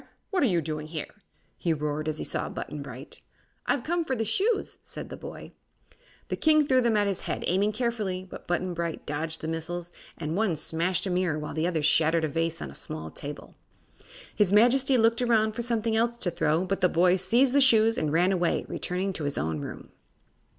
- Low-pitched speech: No, medium, 180 Hz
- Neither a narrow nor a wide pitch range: No, wide, 6.1 semitones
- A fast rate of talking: Yes, fast, 215 wpm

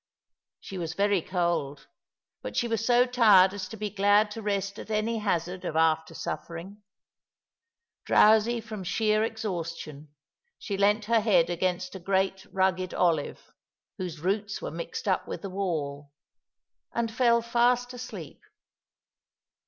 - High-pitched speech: Yes, high, 195 Hz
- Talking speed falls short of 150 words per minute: Yes, average, 140 wpm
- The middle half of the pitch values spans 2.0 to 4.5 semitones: Yes, average, 4.0 semitones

